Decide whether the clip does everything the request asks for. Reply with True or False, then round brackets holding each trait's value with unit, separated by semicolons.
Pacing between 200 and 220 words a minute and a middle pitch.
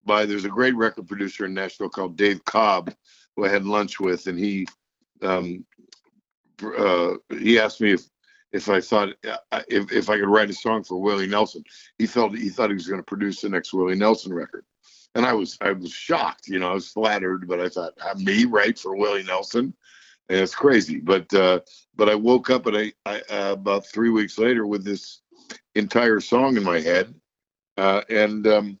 False (205 wpm; 100 Hz)